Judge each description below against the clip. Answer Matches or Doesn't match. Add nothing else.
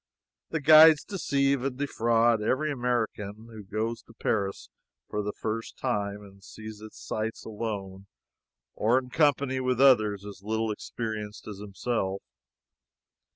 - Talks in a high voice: Doesn't match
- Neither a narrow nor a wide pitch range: Matches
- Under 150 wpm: Matches